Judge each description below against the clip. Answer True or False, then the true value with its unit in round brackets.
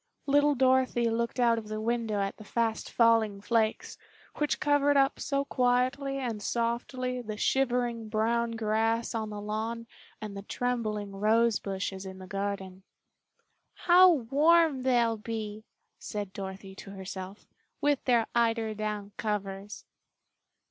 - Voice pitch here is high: True (230 Hz)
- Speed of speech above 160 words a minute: False (135 wpm)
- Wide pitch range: False (3.0 semitones)